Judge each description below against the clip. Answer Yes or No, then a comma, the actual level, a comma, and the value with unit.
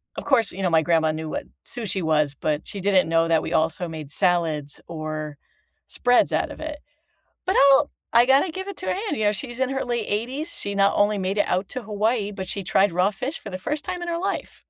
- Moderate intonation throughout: No, wide, 8.0 semitones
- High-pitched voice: Yes, high, 200 Hz